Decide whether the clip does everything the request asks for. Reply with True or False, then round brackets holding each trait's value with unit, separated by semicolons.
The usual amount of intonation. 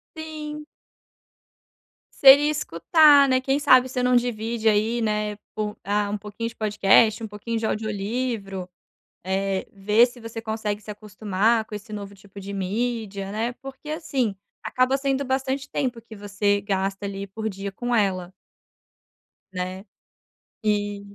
True (3.7 semitones)